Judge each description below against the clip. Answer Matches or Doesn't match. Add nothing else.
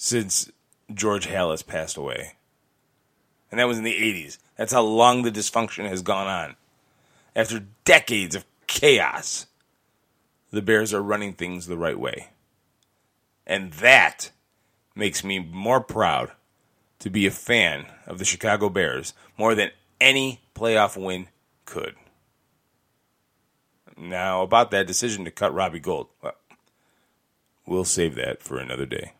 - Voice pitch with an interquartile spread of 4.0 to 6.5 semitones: Doesn't match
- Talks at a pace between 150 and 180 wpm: Doesn't match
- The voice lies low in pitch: Matches